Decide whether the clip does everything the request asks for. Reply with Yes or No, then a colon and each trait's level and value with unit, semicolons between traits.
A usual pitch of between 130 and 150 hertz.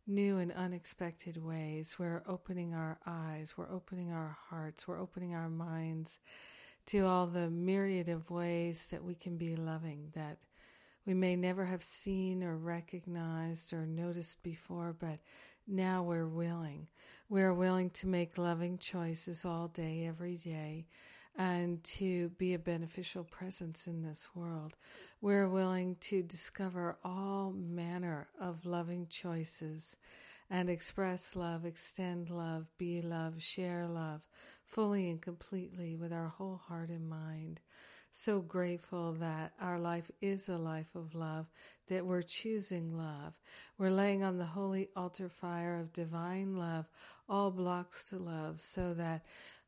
No: medium, 175 Hz